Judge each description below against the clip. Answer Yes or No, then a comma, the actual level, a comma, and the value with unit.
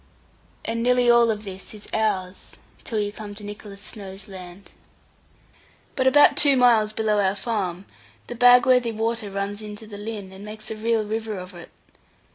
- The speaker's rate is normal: Yes, average, 170 wpm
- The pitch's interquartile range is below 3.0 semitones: Yes, narrow, 2.4 semitones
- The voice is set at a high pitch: Yes, high, 215 Hz